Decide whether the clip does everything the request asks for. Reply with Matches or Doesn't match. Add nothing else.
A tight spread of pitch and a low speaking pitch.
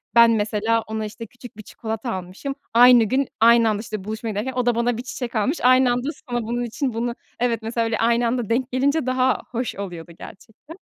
Doesn't match